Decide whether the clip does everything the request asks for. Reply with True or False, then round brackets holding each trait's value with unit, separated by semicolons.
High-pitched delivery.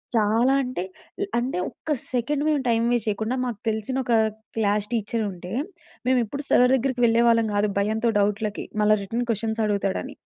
True (225 Hz)